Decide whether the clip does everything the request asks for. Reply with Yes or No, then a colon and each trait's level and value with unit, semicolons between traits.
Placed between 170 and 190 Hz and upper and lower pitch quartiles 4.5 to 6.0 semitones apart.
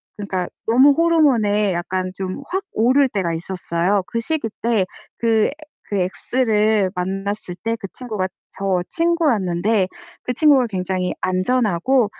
No: high, 210 Hz; average, 5.2 semitones